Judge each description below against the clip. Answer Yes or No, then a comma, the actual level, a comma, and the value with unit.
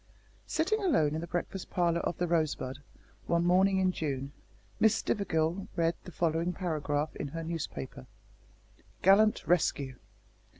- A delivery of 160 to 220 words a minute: No, slow, 135 wpm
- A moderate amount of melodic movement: Yes, average, 3.2 semitones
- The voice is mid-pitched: Yes, medium, 170 Hz